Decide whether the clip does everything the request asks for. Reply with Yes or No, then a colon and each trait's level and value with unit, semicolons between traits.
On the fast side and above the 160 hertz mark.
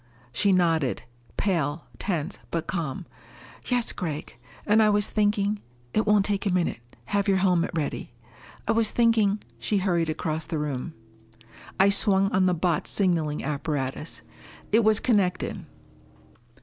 No: average, 150 wpm; medium, 185 Hz